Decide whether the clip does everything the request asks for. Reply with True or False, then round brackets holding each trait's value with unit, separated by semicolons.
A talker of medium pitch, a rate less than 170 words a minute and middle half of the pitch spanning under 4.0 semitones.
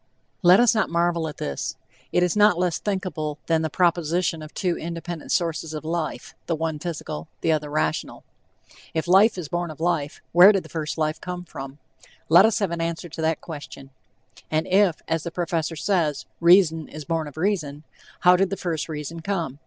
False (165 Hz; 195 wpm; 2.4 semitones)